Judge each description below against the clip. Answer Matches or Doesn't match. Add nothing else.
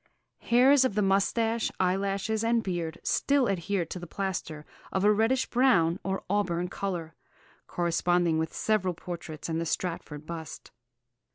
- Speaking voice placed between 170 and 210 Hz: Matches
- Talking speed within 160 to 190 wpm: Doesn't match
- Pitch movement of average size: Matches